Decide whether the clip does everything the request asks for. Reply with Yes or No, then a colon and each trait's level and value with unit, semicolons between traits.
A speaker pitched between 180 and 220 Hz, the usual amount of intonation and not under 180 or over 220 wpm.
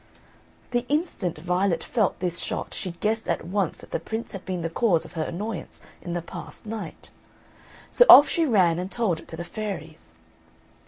Yes: medium, 185 Hz; average, 4.5 semitones; average, 190 wpm